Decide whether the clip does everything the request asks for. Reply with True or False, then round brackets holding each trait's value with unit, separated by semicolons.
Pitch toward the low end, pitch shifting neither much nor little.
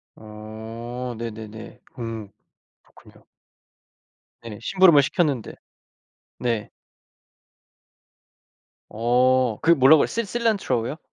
True (120 Hz; 4.4 semitones)